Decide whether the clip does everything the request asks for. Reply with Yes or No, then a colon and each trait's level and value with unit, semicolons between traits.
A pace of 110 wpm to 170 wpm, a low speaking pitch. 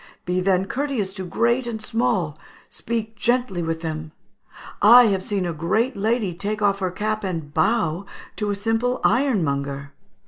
No: average, 160 wpm; high, 200 Hz